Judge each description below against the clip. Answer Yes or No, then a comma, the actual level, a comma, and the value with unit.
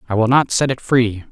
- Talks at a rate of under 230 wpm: No, fast, 275 wpm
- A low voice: Yes, low, 120 Hz